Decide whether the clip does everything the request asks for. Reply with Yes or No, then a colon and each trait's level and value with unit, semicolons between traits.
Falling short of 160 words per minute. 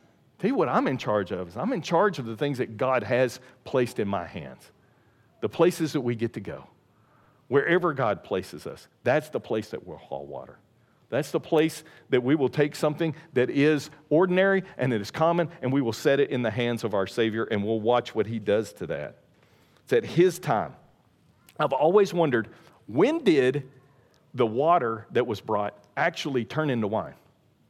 No: average, 195 wpm